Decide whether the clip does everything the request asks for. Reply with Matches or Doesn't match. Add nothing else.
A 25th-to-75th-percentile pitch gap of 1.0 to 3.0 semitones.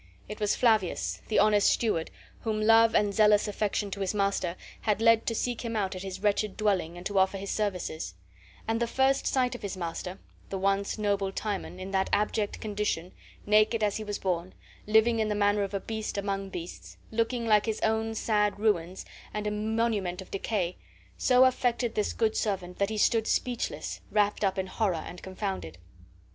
Matches